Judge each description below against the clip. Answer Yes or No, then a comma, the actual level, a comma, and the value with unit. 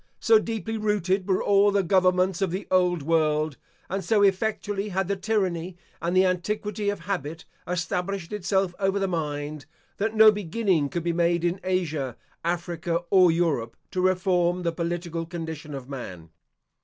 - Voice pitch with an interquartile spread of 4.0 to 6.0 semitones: No, average, 3.0 semitones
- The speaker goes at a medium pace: Yes, average, 160 wpm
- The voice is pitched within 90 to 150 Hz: No, medium, 180 Hz